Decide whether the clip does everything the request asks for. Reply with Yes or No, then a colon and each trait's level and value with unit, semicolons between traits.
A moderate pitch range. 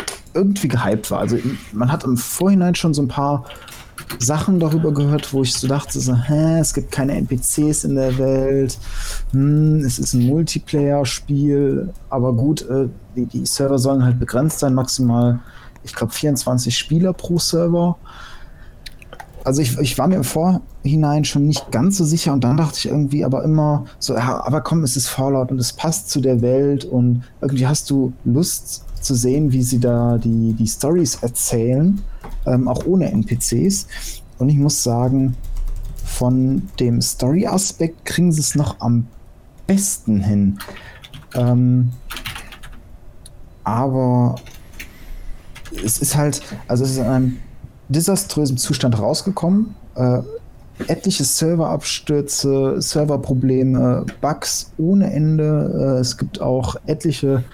Yes: average, 3.5 semitones